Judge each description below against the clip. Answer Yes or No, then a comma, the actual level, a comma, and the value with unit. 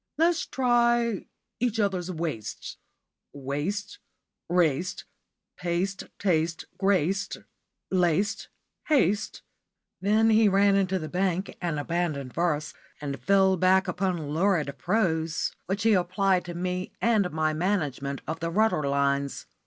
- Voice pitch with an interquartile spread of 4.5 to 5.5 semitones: No, average, 4.1 semitones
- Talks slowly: Yes, slow, 120 wpm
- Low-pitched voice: No, medium, 180 Hz